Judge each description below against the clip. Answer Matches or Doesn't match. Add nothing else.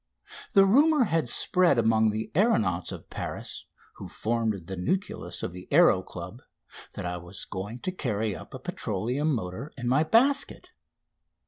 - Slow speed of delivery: Doesn't match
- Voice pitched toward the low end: Matches